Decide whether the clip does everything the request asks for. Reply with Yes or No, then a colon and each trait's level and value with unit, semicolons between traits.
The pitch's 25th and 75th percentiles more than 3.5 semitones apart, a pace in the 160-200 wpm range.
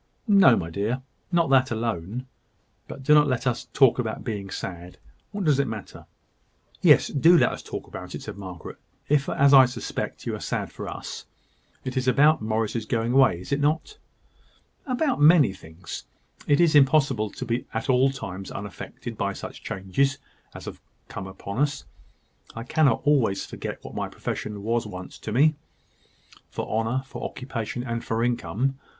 Yes: average, 4.5 semitones; average, 175 wpm